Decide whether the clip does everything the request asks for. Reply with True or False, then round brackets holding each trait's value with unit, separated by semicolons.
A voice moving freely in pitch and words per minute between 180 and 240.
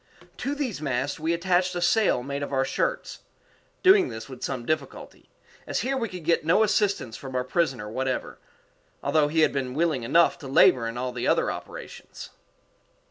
True (5.9 semitones; 185 wpm)